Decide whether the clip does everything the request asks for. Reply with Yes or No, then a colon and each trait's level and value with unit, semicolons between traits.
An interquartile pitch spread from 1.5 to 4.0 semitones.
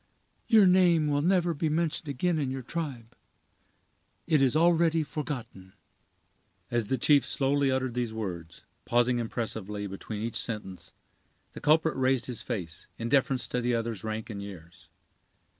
No: wide, 5.6 semitones